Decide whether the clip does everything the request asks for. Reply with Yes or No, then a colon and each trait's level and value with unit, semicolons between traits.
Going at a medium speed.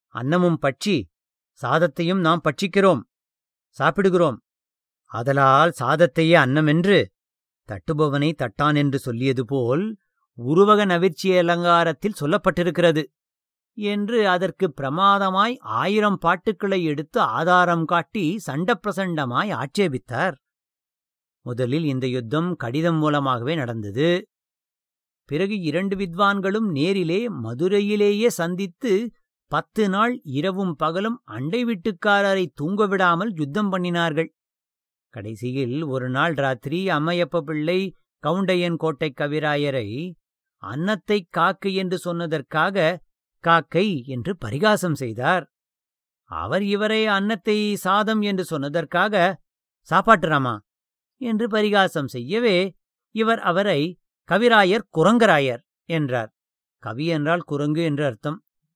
No: slow, 85 wpm